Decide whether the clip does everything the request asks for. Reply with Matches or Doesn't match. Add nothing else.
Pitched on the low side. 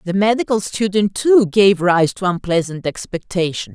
Doesn't match